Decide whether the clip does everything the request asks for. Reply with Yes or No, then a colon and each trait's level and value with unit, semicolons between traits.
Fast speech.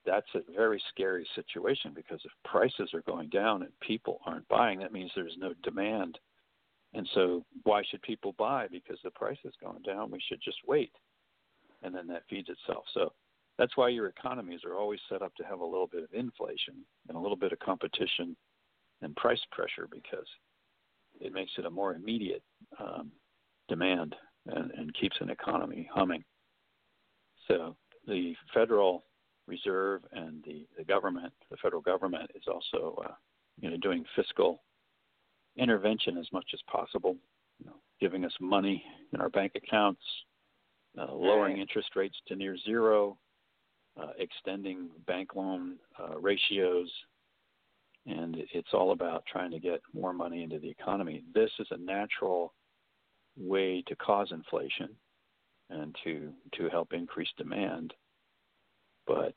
No: average, 155 wpm